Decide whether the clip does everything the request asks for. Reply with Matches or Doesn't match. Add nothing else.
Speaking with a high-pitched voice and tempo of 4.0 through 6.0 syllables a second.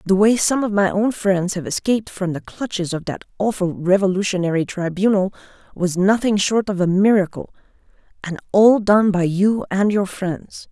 Matches